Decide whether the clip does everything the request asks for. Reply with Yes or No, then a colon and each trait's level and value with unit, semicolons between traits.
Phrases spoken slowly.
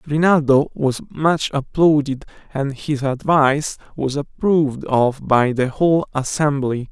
Yes: slow, 120 wpm